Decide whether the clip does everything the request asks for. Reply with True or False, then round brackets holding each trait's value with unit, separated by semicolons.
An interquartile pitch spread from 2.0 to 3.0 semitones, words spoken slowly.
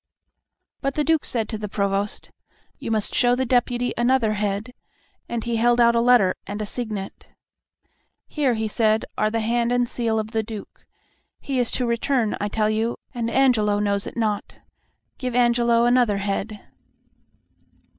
False (2.4 semitones; 165 wpm)